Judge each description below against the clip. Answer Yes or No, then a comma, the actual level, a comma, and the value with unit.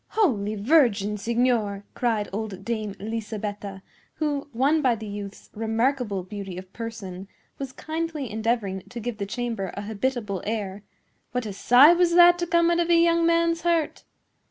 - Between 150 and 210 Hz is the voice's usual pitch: No, high, 230 Hz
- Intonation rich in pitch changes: Yes, wide, 6.3 semitones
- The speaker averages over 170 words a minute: No, average, 160 wpm